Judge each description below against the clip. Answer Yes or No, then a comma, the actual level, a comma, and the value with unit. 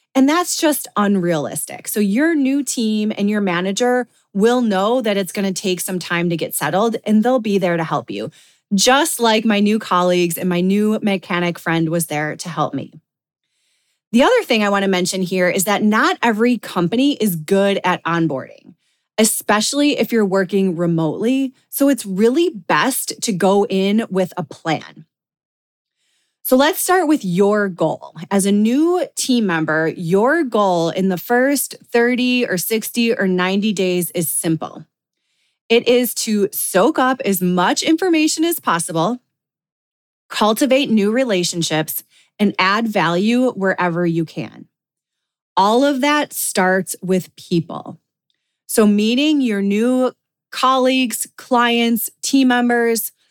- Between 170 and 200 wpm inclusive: No, average, 150 wpm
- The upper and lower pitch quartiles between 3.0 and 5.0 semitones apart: No, wide, 5.4 semitones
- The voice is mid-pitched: No, high, 205 Hz